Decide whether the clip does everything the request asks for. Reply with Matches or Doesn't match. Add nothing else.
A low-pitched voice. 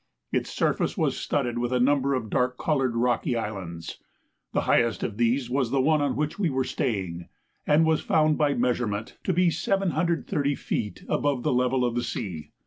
Matches